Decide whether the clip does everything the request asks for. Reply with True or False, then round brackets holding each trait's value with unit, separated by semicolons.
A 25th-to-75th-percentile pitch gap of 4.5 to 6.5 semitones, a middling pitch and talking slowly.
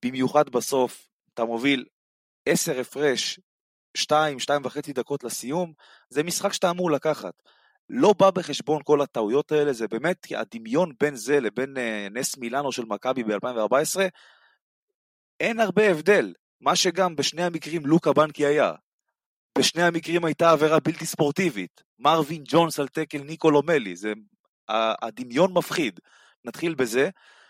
False (5.2 semitones; 150 Hz; 130 wpm)